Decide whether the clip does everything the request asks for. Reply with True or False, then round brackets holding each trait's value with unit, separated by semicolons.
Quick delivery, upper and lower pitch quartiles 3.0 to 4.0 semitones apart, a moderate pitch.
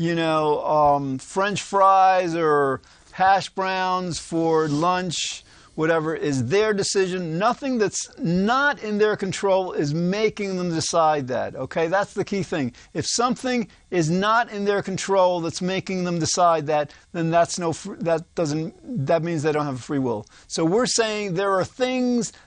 False (165 wpm; 3.6 semitones; 180 Hz)